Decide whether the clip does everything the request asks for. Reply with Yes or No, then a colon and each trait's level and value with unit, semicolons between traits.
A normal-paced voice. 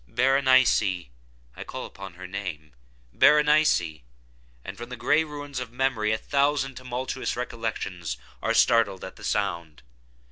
No: slow, 115 wpm